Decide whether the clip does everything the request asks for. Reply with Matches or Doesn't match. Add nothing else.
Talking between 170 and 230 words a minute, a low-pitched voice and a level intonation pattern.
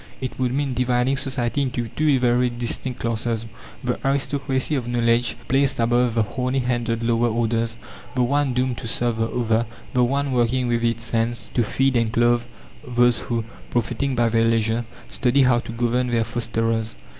Matches